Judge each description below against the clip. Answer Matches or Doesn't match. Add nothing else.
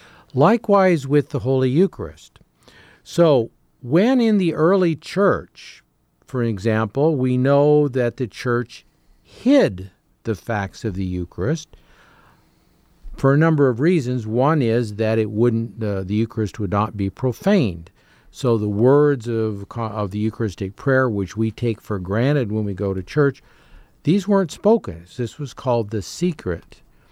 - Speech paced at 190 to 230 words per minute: Doesn't match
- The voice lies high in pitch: Doesn't match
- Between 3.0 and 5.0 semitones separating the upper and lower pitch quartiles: Doesn't match